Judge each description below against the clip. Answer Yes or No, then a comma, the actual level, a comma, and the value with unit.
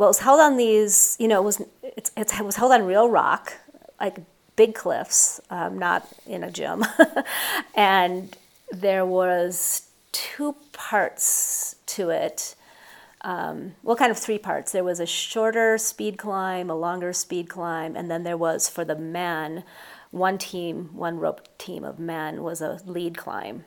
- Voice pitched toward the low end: No, high, 190 Hz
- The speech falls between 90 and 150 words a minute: No, average, 165 wpm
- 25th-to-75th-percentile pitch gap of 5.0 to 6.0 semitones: No, average, 4.3 semitones